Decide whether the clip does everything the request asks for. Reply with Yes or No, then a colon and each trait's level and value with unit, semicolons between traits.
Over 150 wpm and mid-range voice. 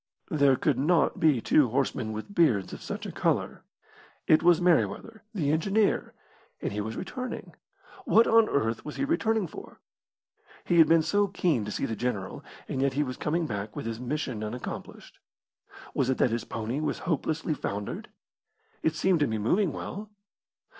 Yes: average, 175 wpm; medium, 150 Hz